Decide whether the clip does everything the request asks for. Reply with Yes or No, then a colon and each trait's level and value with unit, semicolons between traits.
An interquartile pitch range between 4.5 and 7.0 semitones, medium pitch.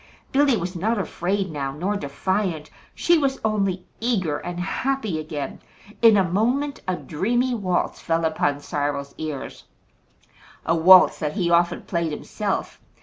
Yes: wide, 5.4 semitones; medium, 180 Hz